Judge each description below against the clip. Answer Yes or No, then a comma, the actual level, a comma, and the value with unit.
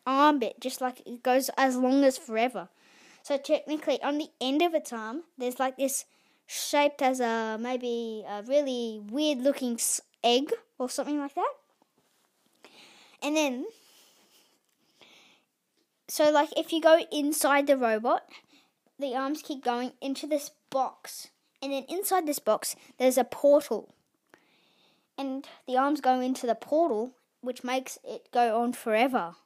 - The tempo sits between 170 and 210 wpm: No, average, 145 wpm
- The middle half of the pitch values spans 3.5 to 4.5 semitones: No, average, 3.1 semitones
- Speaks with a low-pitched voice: No, very high, 270 Hz